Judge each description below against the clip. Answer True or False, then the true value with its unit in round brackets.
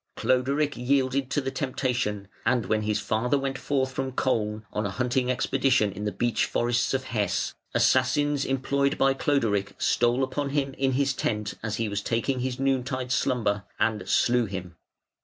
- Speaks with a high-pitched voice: False (125 Hz)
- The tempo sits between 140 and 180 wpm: True (175 wpm)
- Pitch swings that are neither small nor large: True (3.7 semitones)